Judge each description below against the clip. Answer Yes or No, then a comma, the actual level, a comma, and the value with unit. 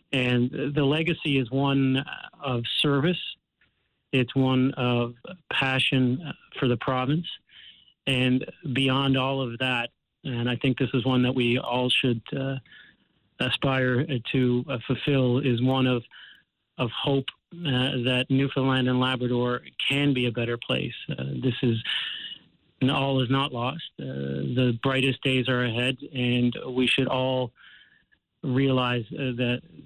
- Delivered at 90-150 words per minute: Yes, average, 145 wpm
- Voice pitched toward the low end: Yes, low, 130 Hz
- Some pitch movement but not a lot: No, narrow, 1.6 semitones